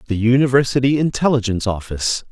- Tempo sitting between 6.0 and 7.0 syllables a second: Yes, 6.7 syllables/s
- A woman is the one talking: No, male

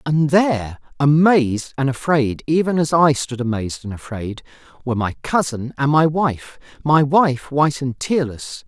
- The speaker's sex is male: Yes, male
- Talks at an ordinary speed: Yes, average, 150 wpm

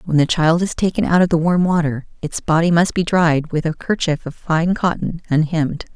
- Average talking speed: No, fast, 220 wpm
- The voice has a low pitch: No, medium, 165 Hz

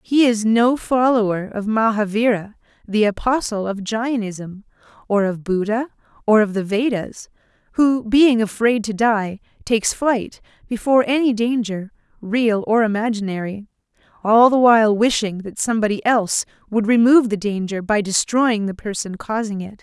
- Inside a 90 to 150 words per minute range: Yes, average, 140 wpm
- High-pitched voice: Yes, high, 220 Hz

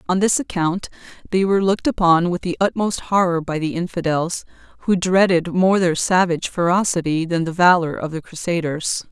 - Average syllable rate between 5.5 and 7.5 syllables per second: No, 5.3 syllables/s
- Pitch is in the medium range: Yes, medium, 175 Hz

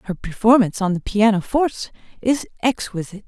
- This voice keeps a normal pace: No, slow, 130 wpm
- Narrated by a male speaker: No, female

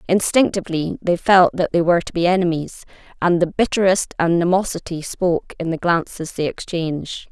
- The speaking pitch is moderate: Yes, medium, 175 Hz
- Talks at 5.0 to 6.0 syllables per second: Yes, 5.4 syllables/s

